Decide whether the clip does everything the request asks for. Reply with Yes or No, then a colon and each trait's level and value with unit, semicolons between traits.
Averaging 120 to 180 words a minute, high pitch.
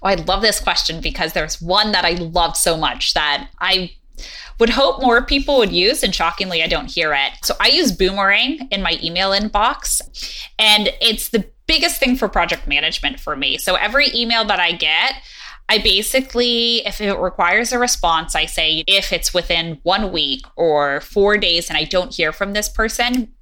No: average, 190 wpm; high, 195 Hz